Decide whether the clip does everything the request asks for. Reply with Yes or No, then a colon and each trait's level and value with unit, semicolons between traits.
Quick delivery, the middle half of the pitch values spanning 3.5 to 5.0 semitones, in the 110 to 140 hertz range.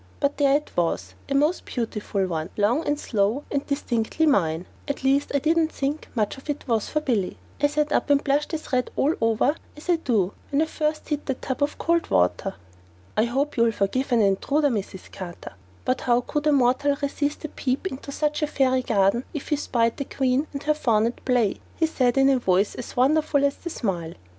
No: fast, 215 wpm; average, 4.5 semitones; very high, 270 Hz